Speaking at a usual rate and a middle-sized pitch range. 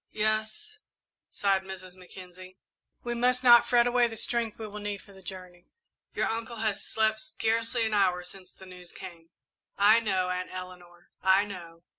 Yes: average, 170 wpm; average, 3.5 semitones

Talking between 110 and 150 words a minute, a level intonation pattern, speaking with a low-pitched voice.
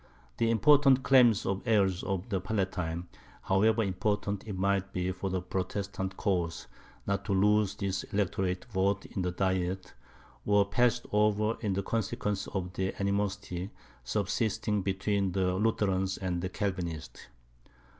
Yes: average, 140 wpm; narrow, 2.0 semitones; very low, 95 Hz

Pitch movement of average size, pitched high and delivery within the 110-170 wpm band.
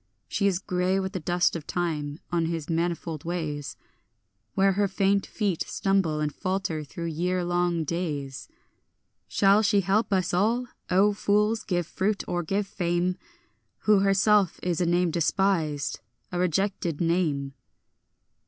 No: average, 3.0 semitones; medium, 180 Hz; average, 145 wpm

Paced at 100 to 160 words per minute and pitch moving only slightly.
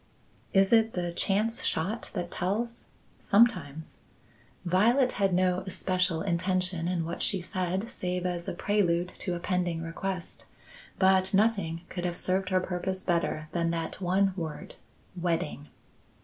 Yes: average, 140 wpm; narrow, 2.1 semitones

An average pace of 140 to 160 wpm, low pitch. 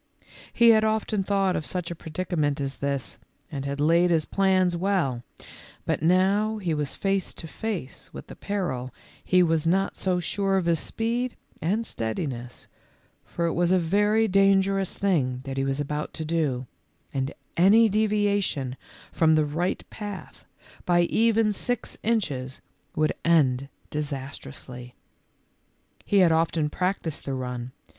No: average, 150 wpm; medium, 170 Hz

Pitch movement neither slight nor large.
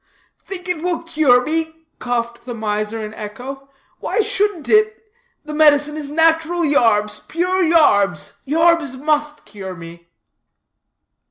No: wide, 6.7 semitones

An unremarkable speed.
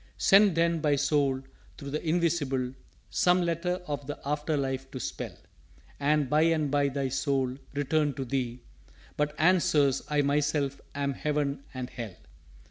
Yes: average, 150 wpm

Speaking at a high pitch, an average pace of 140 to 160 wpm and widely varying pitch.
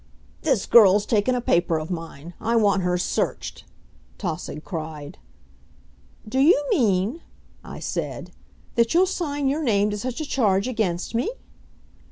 Yes: high, 210 Hz; average, 145 wpm; wide, 6.2 semitones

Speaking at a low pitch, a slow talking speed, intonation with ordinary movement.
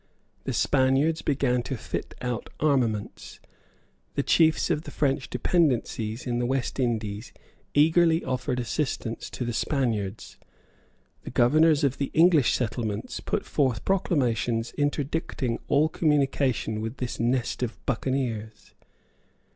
Yes: low, 130 Hz; slow, 125 wpm; average, 3.9 semitones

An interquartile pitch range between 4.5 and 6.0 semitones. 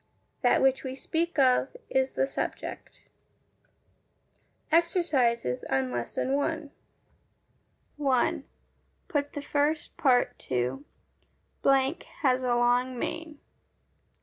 No: average, 3.3 semitones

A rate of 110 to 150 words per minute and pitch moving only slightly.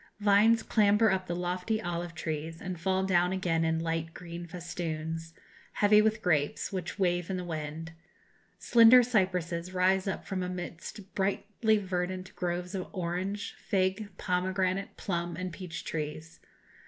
Yes: average, 145 wpm; narrow, 2.3 semitones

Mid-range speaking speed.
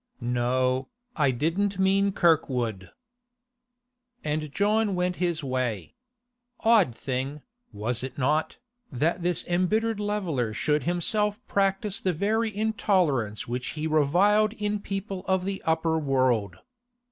No: slow, 120 wpm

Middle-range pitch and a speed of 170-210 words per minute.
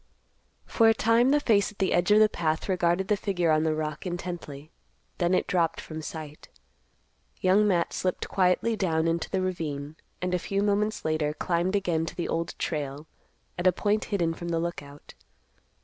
Yes: medium, 175 Hz; average, 185 wpm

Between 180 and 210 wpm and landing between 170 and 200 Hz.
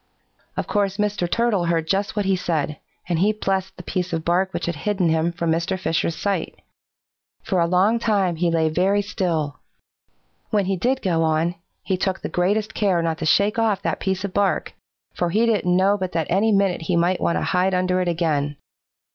Yes: fast, 205 wpm; medium, 185 Hz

